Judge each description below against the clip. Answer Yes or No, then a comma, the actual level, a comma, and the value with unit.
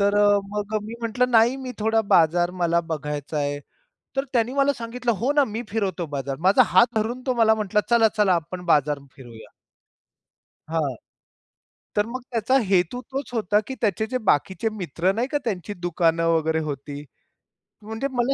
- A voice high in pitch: Yes, high, 210 Hz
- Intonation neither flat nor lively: No, wide, 6.1 semitones